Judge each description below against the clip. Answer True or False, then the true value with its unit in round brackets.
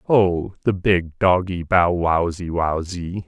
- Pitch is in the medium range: False (90 Hz)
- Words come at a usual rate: False (75 wpm)